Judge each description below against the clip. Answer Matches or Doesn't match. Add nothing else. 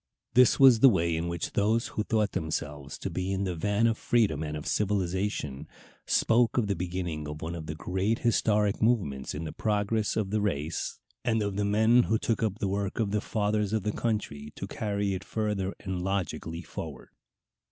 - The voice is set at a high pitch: Doesn't match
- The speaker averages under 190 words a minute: Doesn't match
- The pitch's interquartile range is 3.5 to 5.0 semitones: Matches